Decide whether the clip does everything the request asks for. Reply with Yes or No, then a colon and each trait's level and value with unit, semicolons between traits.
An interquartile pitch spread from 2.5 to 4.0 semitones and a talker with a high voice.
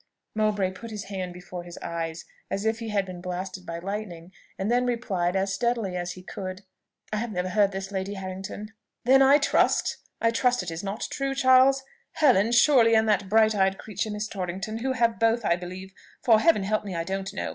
Yes: average, 3.5 semitones; high, 200 Hz